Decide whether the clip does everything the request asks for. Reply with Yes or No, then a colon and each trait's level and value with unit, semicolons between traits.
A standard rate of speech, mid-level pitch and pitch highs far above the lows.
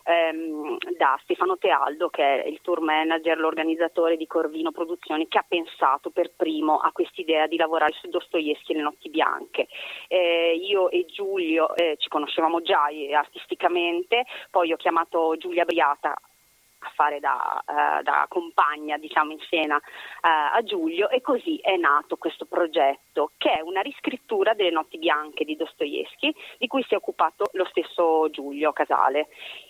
Yes: average, 160 wpm; medium, 170 Hz; wide, 6.8 semitones